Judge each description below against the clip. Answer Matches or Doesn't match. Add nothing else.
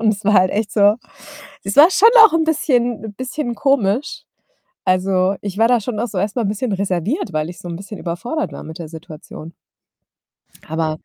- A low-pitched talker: Doesn't match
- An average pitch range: Matches